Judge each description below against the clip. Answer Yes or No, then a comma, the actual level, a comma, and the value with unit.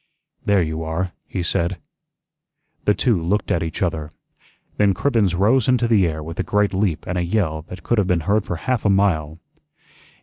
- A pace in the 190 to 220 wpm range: Yes, average, 195 wpm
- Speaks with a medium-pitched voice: No, very low, 95 Hz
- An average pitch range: Yes, average, 3.9 semitones